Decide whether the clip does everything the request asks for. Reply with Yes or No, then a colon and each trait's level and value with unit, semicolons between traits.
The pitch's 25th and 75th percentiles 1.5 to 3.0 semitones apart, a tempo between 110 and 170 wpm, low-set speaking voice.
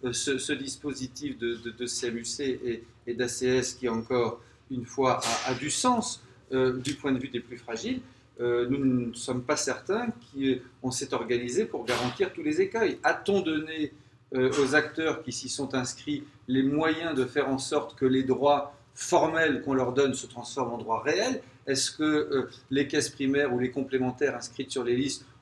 No: narrow, 2.6 semitones; average, 190 wpm; low, 130 Hz